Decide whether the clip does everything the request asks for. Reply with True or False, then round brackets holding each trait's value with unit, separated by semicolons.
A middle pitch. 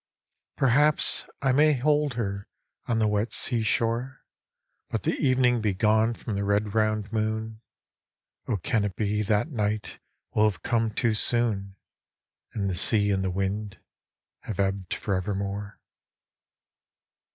False (110 Hz)